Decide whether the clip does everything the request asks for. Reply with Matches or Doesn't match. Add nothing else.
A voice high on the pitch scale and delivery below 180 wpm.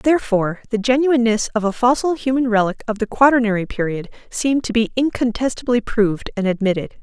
Matches